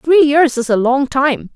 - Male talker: No, female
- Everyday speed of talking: No, fast, 230 wpm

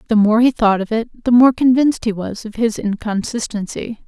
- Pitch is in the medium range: No, high, 225 Hz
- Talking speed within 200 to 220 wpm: Yes, fast, 205 wpm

